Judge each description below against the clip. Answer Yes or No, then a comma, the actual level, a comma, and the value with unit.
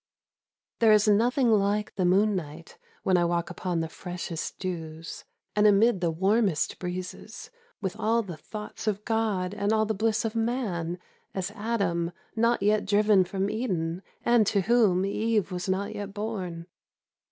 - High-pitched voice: Yes, high, 200 Hz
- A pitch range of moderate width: Yes, average, 3.4 semitones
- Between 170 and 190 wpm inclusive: No, average, 160 wpm